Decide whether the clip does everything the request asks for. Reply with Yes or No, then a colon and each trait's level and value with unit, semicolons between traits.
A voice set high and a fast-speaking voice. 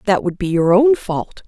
Yes: high, 195 Hz; fast, 245 wpm